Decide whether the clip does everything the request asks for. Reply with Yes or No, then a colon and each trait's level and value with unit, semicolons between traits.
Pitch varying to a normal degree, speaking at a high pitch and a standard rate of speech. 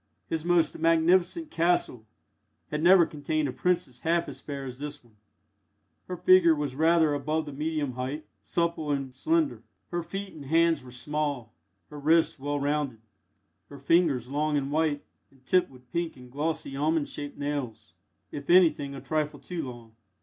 No: average, 3.3 semitones; medium, 150 Hz; average, 165 wpm